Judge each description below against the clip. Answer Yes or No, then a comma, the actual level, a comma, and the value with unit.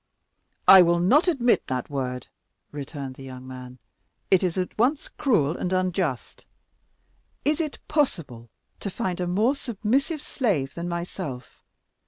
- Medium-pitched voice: Yes, medium, 180 Hz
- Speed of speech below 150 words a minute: Yes, average, 140 wpm